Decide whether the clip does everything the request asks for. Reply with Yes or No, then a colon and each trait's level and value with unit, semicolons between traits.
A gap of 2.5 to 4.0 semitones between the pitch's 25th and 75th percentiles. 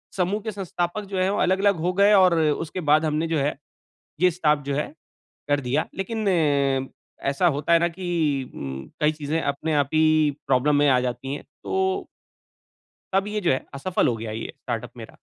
No: average, 5.0 semitones